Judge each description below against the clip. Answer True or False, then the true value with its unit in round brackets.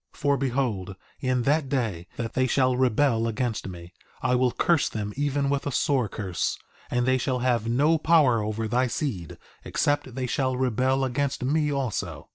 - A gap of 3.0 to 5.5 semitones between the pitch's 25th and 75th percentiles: True (3.5 semitones)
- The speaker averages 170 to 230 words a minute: True (180 wpm)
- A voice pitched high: False (130 Hz)